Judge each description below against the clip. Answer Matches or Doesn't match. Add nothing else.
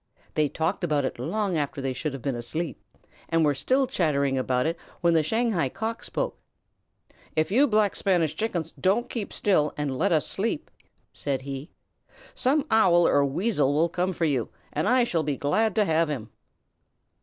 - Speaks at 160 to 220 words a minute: Matches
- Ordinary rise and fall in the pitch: Doesn't match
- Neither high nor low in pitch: Matches